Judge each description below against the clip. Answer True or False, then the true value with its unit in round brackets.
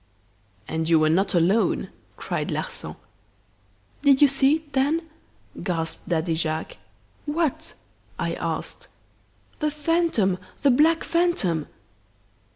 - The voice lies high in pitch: True (270 Hz)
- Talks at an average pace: False (110 wpm)